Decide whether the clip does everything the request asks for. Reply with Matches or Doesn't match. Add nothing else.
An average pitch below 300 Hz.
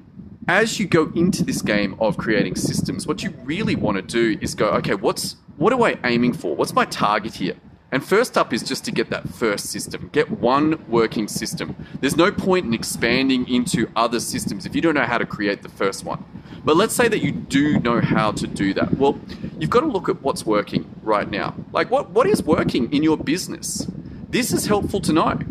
Matches